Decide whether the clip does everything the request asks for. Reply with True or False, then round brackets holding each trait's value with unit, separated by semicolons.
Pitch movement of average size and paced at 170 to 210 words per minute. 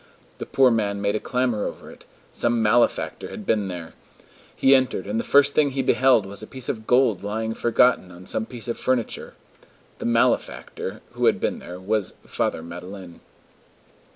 True (4.0 semitones; 180 wpm)